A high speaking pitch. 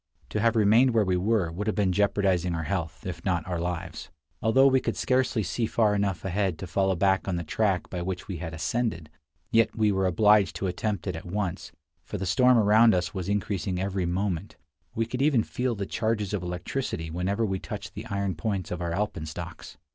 No: low, 100 Hz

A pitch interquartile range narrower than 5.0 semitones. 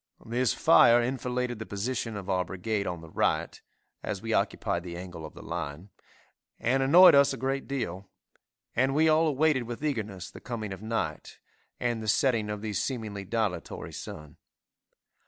No: average, 5.3 semitones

